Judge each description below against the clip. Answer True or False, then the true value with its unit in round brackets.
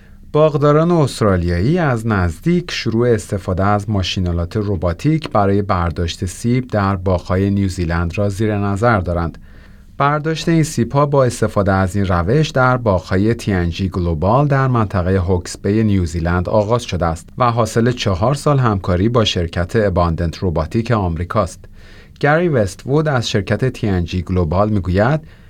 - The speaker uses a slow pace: False (135 wpm)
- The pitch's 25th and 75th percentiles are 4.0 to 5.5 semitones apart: True (4.8 semitones)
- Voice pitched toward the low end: True (105 Hz)